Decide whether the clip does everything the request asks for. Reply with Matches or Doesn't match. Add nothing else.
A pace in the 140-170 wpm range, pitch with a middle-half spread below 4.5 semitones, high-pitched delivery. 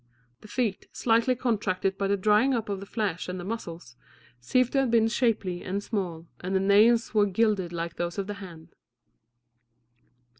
Doesn't match